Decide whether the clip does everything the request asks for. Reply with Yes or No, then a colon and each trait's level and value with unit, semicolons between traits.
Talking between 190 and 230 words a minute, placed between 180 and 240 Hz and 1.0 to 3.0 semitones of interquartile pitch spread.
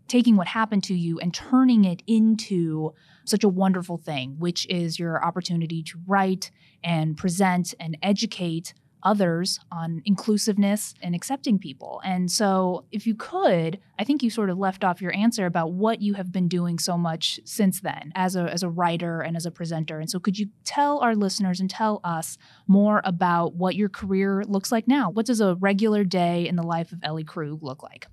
No: average, 200 wpm; medium, 185 Hz; average, 3.4 semitones